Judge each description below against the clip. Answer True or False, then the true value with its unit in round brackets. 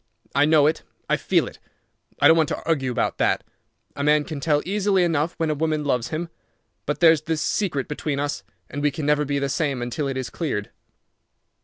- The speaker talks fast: True (210 wpm)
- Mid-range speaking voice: True (150 Hz)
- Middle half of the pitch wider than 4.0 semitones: False (2.4 semitones)